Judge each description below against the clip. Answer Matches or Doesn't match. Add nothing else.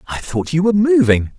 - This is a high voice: Doesn't match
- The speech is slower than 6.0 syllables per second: Matches